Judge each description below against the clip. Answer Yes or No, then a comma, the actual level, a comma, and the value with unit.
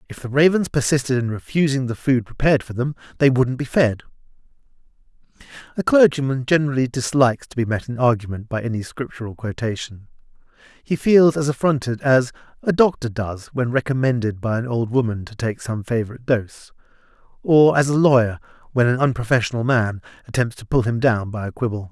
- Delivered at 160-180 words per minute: Yes, average, 170 wpm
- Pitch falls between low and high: No, low, 125 Hz